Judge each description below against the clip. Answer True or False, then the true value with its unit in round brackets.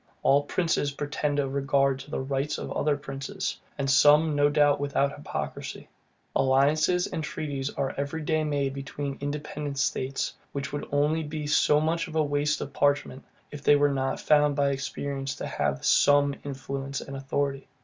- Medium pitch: True (145 Hz)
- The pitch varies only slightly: True (1.2 semitones)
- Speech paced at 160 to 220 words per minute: True (165 wpm)